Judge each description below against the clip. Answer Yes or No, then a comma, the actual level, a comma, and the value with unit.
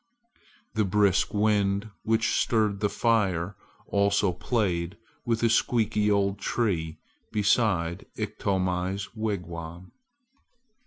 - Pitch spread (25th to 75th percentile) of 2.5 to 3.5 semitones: Yes, average, 2.8 semitones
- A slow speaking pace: Yes, slow, 95 wpm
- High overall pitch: No, low, 100 Hz